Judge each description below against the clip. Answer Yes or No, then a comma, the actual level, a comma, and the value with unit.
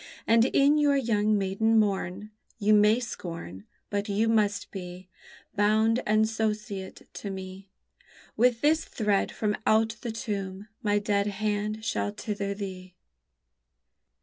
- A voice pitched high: Yes, high, 210 Hz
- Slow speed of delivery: Yes, slow, 130 wpm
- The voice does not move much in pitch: Yes, narrow, 2.0 semitones